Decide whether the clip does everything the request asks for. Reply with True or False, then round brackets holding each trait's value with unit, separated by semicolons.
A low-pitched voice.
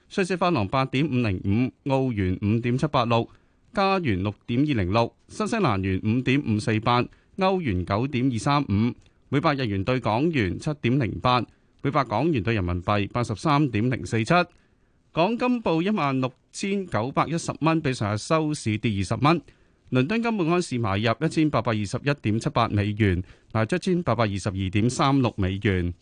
True (125 Hz)